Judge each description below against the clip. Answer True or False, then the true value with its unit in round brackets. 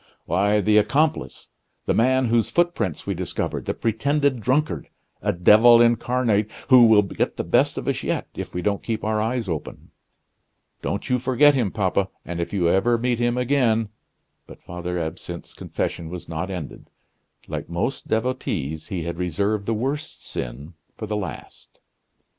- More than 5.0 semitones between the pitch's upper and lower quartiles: True (5.6 semitones)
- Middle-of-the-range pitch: False (110 Hz)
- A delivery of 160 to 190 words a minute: True (165 wpm)